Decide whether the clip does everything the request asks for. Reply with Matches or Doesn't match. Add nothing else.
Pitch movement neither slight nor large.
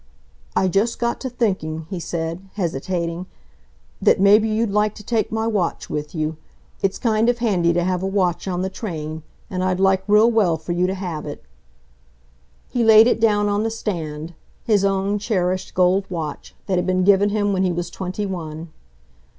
Matches